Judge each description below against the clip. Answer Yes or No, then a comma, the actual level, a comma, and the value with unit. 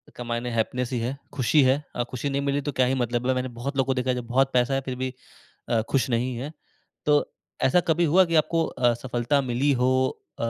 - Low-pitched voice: Yes, low, 130 Hz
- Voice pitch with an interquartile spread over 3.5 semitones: No, narrow, 2.4 semitones